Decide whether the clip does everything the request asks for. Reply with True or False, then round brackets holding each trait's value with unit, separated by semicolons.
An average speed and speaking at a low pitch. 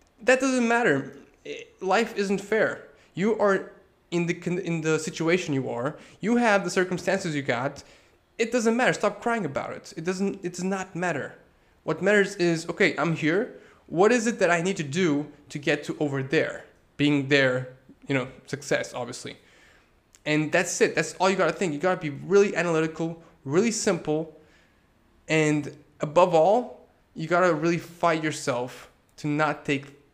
False (170 wpm; 170 Hz)